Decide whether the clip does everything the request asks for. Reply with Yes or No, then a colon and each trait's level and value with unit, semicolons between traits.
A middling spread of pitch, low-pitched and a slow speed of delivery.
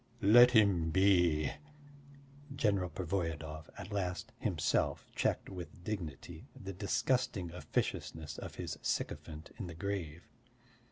Yes: average, 3.6 semitones; very low, 90 Hz; slow, 110 wpm